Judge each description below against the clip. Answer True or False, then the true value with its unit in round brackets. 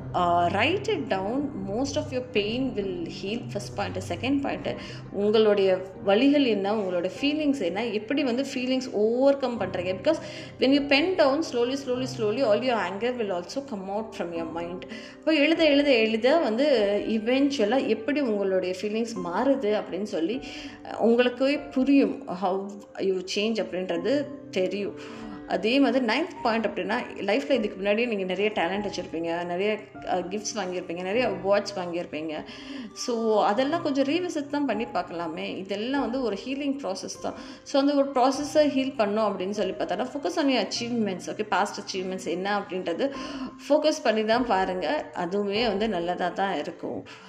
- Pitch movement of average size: False (5.8 semitones)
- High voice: True (220 Hz)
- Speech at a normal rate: False (150 wpm)